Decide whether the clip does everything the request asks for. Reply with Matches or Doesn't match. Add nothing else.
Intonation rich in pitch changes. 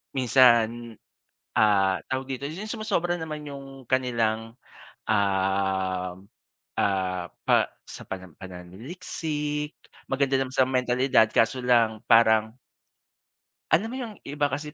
Matches